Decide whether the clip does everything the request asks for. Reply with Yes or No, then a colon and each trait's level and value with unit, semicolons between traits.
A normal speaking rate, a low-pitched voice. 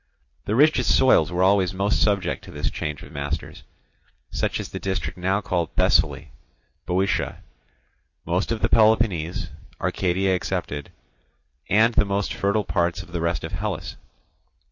Yes: average, 145 wpm; very low, 95 Hz